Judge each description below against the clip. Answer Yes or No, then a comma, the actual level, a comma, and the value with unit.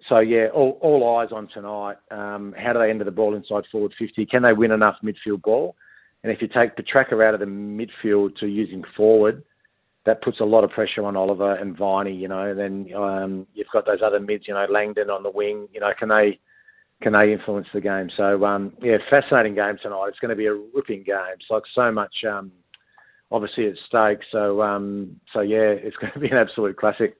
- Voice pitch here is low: Yes, low, 105 Hz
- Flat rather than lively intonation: Yes, narrow, 1.5 semitones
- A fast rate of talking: Yes, fast, 225 wpm